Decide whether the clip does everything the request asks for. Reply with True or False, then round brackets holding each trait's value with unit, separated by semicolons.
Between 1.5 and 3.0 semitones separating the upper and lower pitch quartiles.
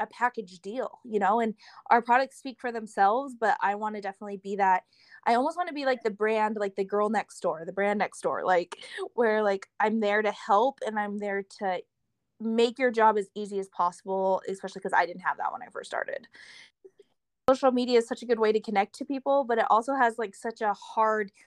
False (3.4 semitones)